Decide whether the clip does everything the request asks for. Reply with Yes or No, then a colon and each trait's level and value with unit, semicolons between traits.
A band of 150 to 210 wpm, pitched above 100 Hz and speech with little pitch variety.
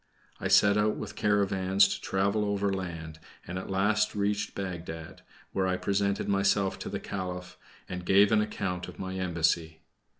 No: average, 160 wpm; very low, 95 Hz; narrow, 2.0 semitones